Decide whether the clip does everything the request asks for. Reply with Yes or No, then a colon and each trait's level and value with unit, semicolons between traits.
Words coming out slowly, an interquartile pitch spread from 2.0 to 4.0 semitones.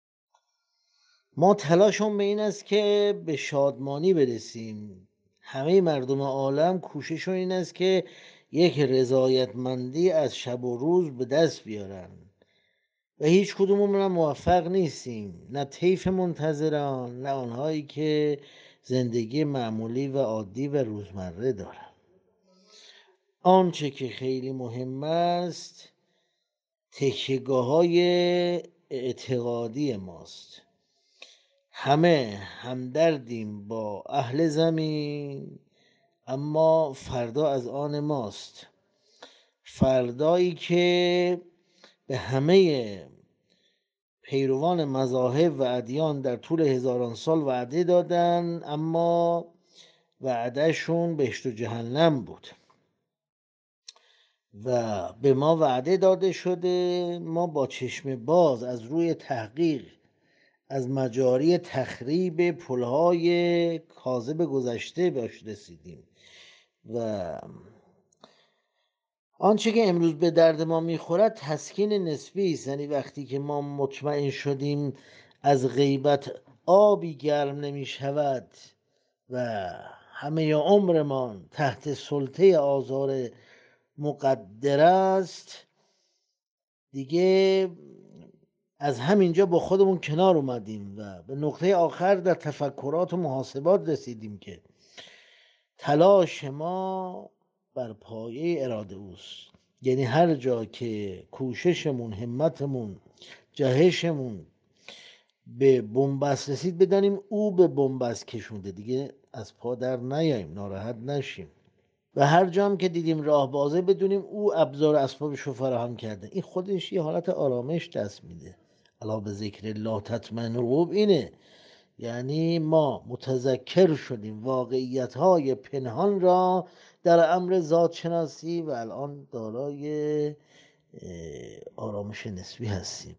No: slow, 100 wpm; wide, 5.4 semitones